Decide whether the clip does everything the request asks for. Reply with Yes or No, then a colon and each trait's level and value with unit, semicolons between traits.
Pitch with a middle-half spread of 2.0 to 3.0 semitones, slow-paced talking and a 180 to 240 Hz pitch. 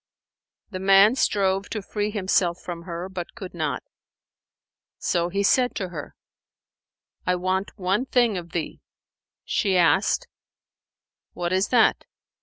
Yes: average, 2.7 semitones; slow, 130 wpm; high, 190 Hz